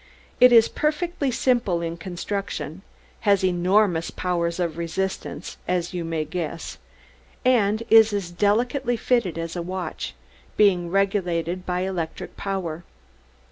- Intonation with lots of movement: No, average, 3.9 semitones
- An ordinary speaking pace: No, slow, 125 wpm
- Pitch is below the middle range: No, medium, 185 Hz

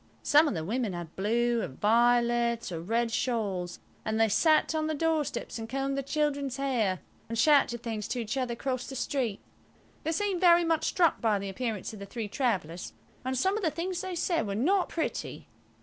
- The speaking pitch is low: No, high, 240 Hz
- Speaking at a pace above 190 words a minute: Yes, average, 200 wpm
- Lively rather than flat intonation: Yes, wide, 5.7 semitones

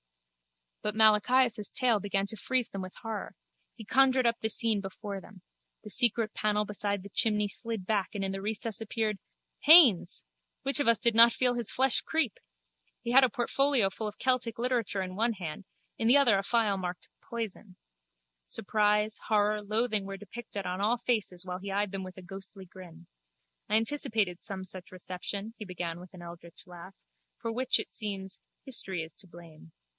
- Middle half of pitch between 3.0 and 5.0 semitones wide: Yes, average, 3.4 semitones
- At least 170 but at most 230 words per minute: Yes, average, 185 wpm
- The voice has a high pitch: Yes, high, 210 Hz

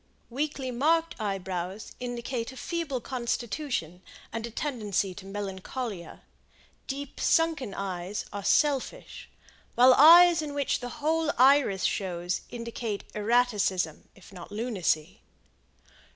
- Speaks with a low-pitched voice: No, high, 235 Hz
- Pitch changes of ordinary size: No, wide, 6.2 semitones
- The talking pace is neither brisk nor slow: No, slow, 110 wpm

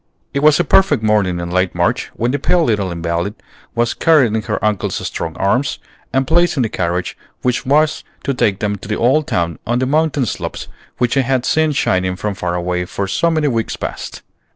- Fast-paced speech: Yes, fast, 210 wpm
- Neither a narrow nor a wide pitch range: No, wide, 7.2 semitones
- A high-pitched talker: No, low, 115 Hz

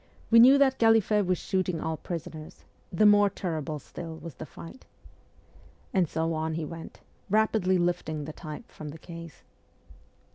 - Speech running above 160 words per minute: No, average, 155 wpm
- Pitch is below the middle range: No, medium, 170 Hz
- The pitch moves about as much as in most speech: Yes, average, 4.5 semitones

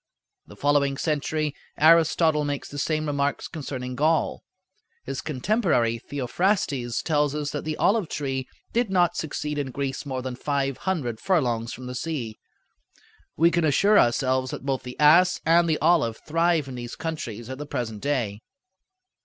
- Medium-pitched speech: Yes, medium, 145 Hz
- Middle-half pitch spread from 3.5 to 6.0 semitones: Yes, average, 3.9 semitones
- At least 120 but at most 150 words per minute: No, average, 160 wpm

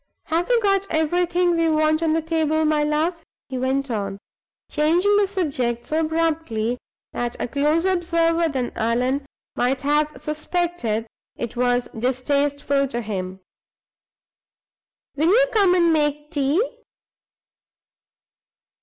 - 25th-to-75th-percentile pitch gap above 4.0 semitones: Yes, average, 4.5 semitones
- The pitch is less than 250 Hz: No, very high, 300 Hz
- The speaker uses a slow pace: Yes, slow, 125 wpm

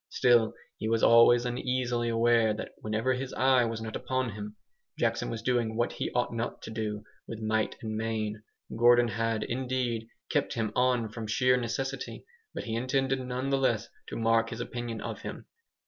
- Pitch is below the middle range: Yes, low, 115 Hz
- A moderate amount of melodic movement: No, narrow, 2.1 semitones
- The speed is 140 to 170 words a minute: No, average, 180 wpm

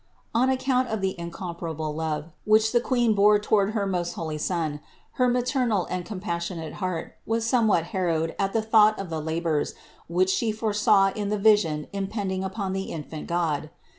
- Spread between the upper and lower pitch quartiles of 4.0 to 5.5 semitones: Yes, average, 4.4 semitones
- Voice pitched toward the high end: Yes, high, 195 Hz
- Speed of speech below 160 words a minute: No, average, 175 wpm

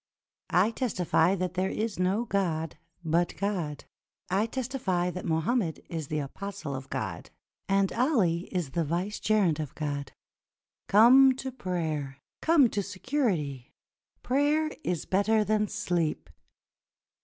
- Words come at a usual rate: No, slow, 125 wpm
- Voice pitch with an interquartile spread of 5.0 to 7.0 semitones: Yes, average, 5.3 semitones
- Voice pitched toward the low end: No, medium, 185 Hz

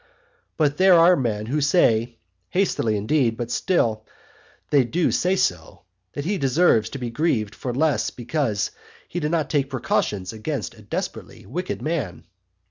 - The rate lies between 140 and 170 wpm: Yes, average, 155 wpm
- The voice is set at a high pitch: No, low, 135 Hz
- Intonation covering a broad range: Yes, wide, 6.4 semitones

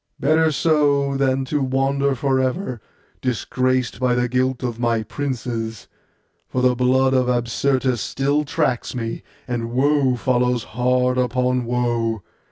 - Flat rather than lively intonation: Yes, narrow, 1.8 semitones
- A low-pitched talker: Yes, low, 125 Hz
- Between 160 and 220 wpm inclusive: No, slow, 135 wpm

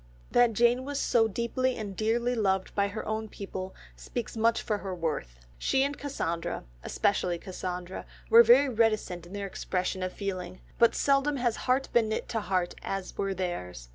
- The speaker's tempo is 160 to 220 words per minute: Yes, average, 175 wpm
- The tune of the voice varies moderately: Yes, average, 4.4 semitones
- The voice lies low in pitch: No, high, 210 Hz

